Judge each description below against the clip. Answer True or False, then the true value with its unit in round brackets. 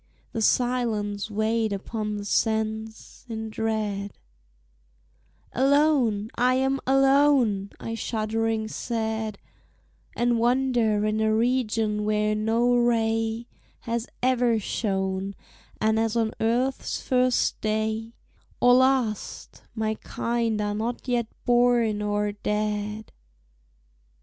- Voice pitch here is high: True (225 Hz)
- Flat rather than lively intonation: True (2.2 semitones)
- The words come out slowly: True (105 wpm)